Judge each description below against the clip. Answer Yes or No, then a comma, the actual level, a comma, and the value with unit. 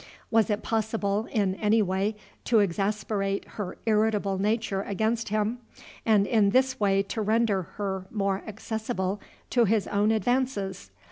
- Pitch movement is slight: Yes, narrow, 2.0 semitones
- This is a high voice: Yes, high, 210 Hz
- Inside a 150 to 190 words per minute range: No, average, 140 wpm